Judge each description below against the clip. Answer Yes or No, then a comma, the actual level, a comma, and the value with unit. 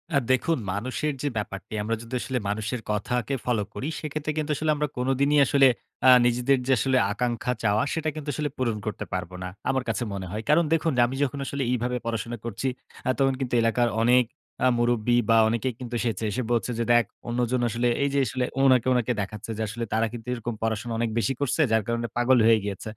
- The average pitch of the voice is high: No, low, 120 Hz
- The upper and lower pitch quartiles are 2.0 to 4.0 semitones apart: Yes, average, 2.9 semitones